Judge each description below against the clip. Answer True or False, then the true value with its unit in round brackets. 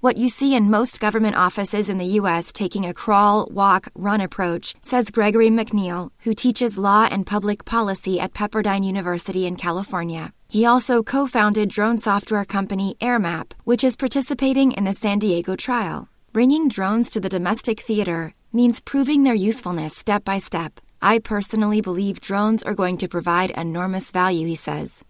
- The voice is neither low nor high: False (205 Hz)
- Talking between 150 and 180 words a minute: True (170 wpm)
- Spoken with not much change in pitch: False (3.4 semitones)